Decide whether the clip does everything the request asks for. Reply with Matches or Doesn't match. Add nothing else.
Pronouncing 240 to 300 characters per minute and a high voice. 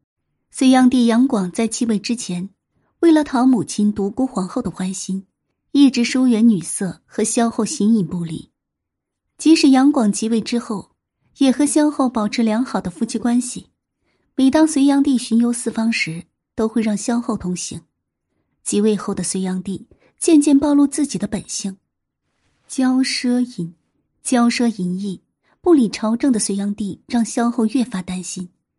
Doesn't match